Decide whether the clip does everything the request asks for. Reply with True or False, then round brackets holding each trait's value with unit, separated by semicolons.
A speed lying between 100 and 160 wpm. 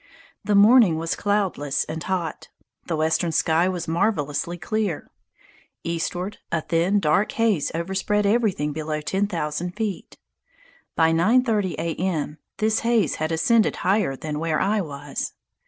True (140 wpm)